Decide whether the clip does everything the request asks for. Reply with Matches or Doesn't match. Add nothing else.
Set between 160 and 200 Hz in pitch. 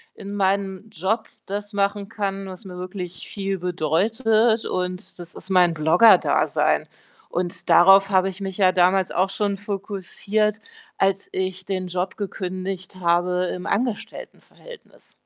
Matches